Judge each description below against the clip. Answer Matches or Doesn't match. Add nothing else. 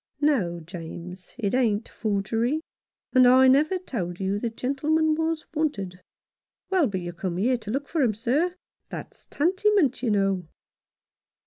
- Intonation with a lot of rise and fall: Matches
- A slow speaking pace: Doesn't match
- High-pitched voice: Matches